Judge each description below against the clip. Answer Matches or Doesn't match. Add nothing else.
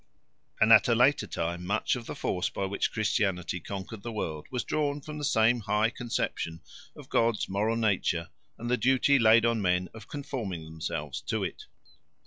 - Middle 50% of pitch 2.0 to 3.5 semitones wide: Doesn't match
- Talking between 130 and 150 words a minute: Doesn't match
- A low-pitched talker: Matches